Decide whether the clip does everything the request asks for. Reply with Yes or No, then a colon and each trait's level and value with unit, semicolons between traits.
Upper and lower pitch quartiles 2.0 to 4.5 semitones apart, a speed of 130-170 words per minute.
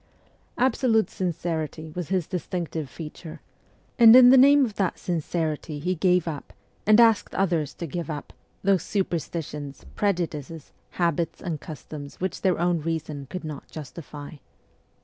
Yes: average, 3.5 semitones; average, 150 wpm